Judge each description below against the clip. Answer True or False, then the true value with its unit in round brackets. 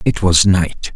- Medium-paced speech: True (190 wpm)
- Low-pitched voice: True (95 Hz)